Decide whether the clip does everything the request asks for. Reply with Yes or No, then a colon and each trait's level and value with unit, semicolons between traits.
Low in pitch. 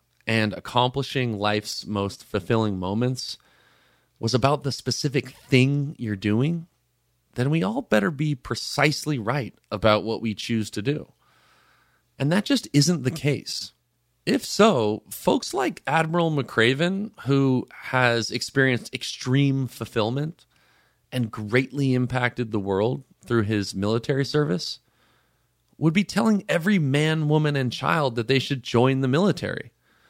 Yes: low, 130 Hz